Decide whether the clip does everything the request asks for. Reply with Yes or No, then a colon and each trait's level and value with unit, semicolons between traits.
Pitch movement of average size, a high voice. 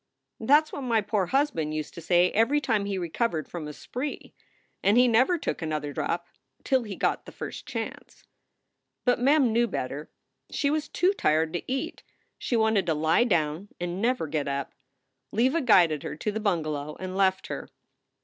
No: wide, 7.5 semitones; high, 200 Hz